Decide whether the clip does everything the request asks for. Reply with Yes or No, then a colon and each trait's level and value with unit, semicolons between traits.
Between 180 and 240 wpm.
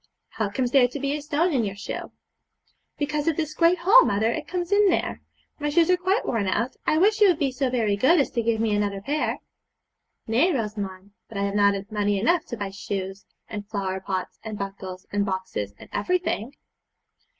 Yes: fast, 205 wpm